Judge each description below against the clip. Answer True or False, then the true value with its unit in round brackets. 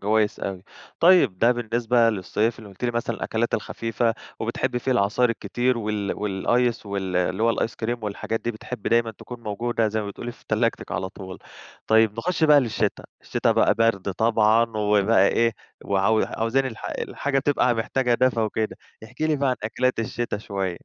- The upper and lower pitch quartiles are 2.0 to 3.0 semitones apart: True (2.4 semitones)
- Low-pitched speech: True (115 Hz)